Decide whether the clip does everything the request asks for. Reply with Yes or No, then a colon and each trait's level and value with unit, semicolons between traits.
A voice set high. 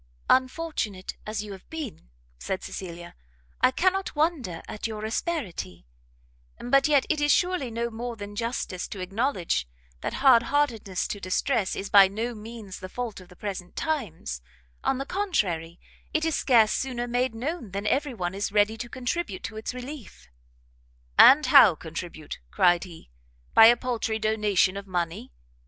Yes: high, 220 Hz